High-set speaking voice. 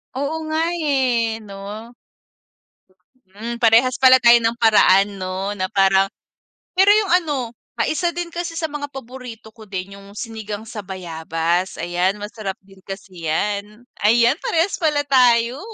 Yes: high, 225 Hz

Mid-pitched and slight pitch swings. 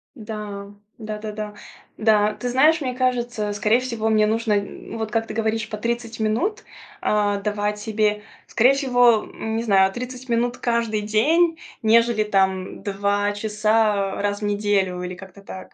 No: high, 215 Hz; narrow, 2.3 semitones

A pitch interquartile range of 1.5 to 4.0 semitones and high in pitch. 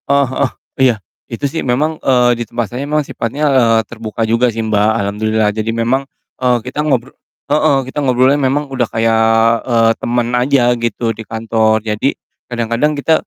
No: average, 3.1 semitones; low, 120 Hz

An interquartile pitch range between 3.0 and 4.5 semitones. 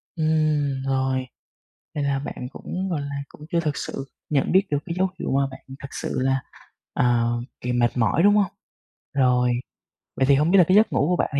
Yes: average, 4.1 semitones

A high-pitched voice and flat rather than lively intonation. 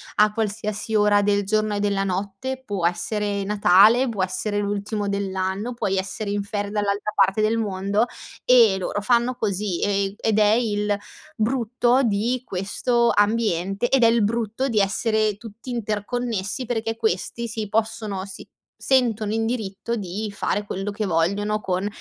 Yes: high, 210 Hz; narrow, 2.1 semitones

